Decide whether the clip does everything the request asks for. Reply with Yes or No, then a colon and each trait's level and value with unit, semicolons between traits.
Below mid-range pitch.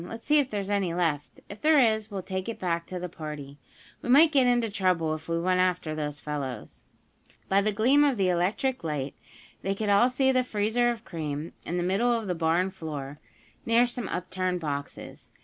No: medium, 185 Hz